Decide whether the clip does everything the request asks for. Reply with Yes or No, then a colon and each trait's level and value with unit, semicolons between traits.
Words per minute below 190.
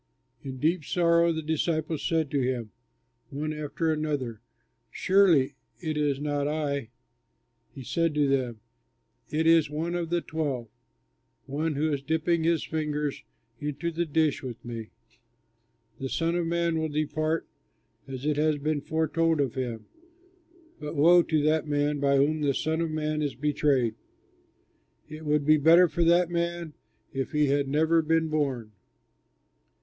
Yes: average, 155 wpm